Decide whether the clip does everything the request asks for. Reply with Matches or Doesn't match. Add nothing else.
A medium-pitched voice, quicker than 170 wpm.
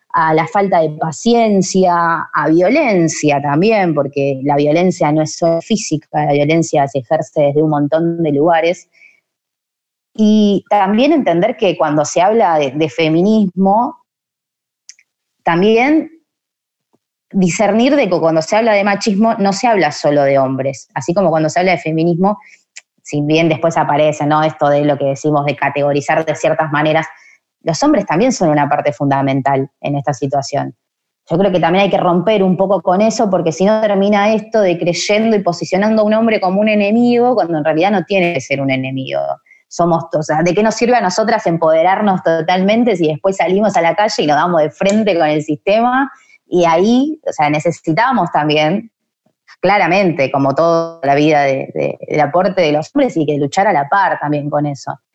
Matches